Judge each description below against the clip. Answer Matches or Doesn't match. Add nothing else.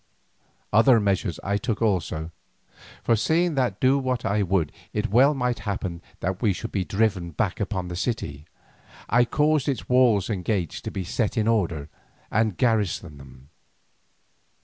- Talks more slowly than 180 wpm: Matches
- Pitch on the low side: Matches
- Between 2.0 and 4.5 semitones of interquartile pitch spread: Doesn't match